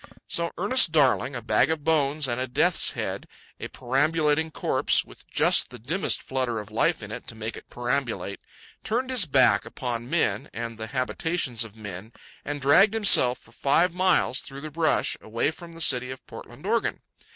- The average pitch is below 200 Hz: Yes, low, 135 Hz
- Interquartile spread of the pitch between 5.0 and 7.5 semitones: Yes, wide, 5.5 semitones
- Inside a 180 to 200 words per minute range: Yes, average, 185 wpm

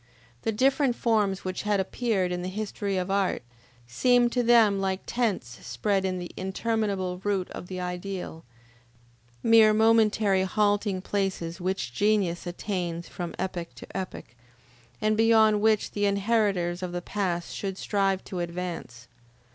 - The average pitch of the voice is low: No, high, 195 Hz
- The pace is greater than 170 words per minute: No, average, 145 wpm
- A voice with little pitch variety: No, average, 3.0 semitones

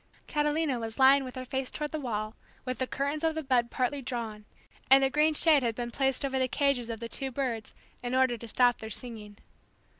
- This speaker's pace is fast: Yes, fast, 220 wpm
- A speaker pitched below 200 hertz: No, very high, 260 Hz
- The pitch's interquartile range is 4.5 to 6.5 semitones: No, average, 2.8 semitones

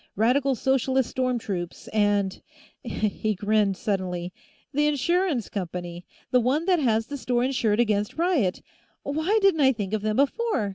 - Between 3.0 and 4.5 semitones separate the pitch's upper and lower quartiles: No, wide, 5.5 semitones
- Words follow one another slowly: No, average, 155 wpm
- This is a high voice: Yes, high, 235 Hz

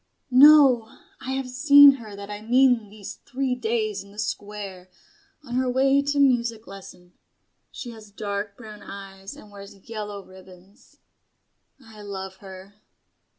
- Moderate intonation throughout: Yes, average, 4.1 semitones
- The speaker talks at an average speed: Yes, average, 145 wpm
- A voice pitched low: No, high, 215 Hz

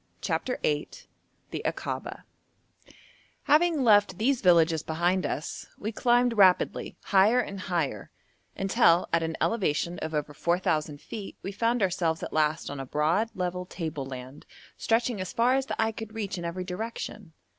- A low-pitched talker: No, medium, 185 Hz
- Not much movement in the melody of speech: No, wide, 5.6 semitones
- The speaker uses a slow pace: No, average, 155 wpm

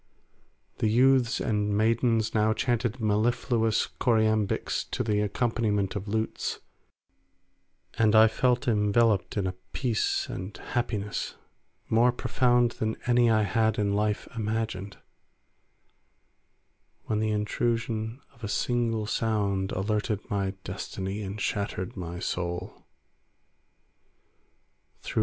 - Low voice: Yes, low, 110 Hz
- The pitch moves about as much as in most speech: No, narrow, 2.1 semitones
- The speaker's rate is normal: No, slow, 105 wpm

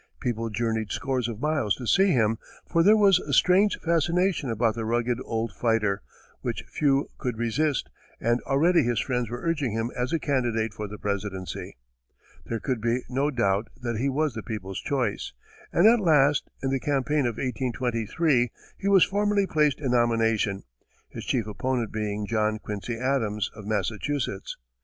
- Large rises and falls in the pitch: No, average, 4.6 semitones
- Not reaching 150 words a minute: No, average, 170 wpm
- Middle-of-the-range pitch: No, low, 120 Hz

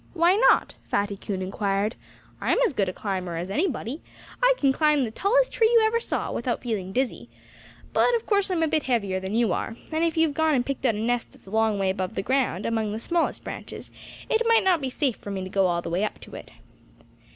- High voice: Yes, high, 240 Hz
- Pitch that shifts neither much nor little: No, wide, 8.5 semitones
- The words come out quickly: Yes, fast, 240 wpm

